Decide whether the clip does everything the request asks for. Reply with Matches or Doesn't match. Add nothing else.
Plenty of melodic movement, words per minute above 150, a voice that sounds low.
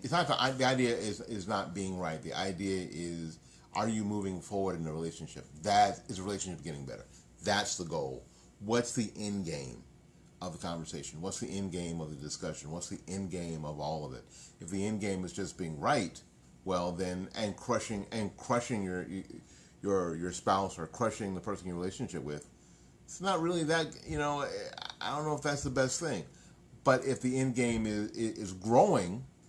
Matches